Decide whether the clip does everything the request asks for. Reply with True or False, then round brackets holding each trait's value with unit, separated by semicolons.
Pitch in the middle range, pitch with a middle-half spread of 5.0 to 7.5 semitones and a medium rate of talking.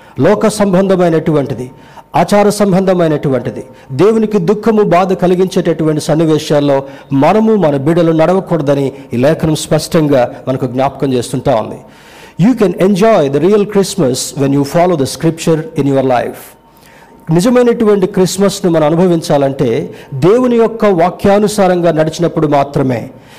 True (165 Hz; 5.4 semitones; 110 wpm)